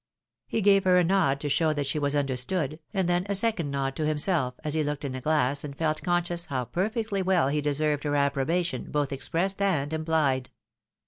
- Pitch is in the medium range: Yes, medium, 155 Hz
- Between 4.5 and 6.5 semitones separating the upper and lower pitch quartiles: No, average, 4.0 semitones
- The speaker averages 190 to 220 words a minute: Yes, fast, 205 wpm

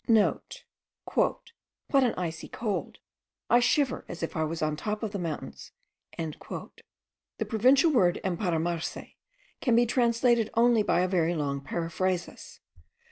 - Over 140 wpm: No, slow, 135 wpm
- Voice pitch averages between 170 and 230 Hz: Yes, high, 190 Hz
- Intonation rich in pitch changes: Yes, wide, 6.0 semitones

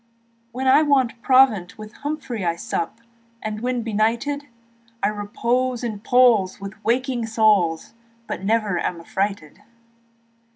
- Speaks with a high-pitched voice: Yes, high, 225 Hz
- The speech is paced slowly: Yes, slow, 125 wpm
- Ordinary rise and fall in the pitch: Yes, average, 3.9 semitones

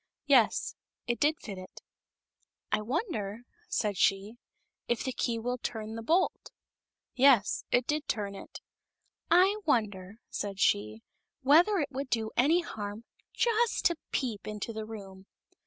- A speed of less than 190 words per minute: Yes, average, 160 wpm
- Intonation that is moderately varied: No, wide, 5.8 semitones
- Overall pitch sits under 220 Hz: No, high, 230 Hz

